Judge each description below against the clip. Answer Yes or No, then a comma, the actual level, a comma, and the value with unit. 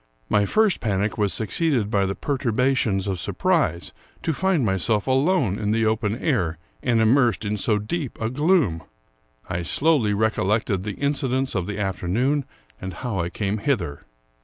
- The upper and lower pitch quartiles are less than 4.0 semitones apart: No, average, 5.3 semitones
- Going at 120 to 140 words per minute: No, average, 165 wpm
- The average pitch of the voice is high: No, low, 110 Hz